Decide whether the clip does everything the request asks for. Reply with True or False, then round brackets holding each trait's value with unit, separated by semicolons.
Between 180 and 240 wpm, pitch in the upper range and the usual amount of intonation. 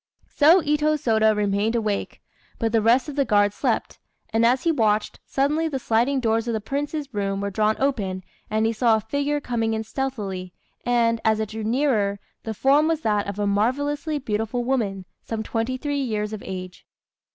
True (190 wpm; 225 Hz; 4.4 semitones)